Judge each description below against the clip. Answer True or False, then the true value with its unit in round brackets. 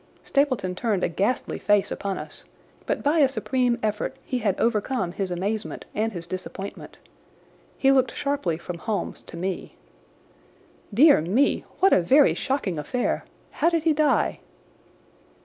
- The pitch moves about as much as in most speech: False (6.5 semitones)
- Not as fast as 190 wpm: True (150 wpm)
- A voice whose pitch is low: False (220 Hz)